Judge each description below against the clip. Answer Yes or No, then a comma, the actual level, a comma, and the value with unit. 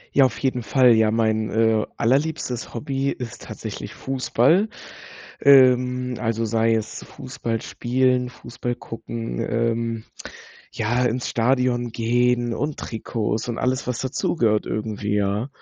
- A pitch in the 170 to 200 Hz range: No, low, 120 Hz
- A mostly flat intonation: Yes, narrow, 2.0 semitones